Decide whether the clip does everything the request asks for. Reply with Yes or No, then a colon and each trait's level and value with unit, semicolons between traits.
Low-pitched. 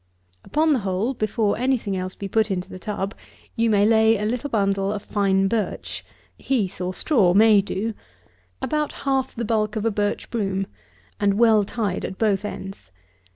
No: high, 210 Hz